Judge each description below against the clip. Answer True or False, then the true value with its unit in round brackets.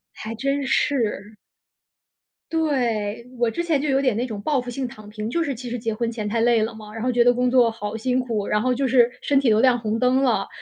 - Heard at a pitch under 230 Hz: False (240 Hz)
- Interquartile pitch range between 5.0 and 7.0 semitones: False (2.9 semitones)